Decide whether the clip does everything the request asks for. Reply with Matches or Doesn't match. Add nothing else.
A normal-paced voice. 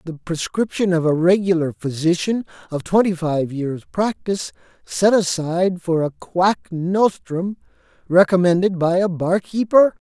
Doesn't match